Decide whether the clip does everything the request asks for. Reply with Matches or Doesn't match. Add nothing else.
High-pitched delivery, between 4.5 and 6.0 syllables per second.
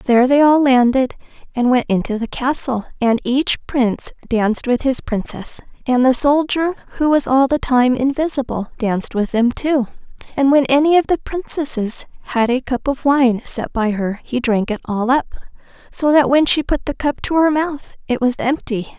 Matches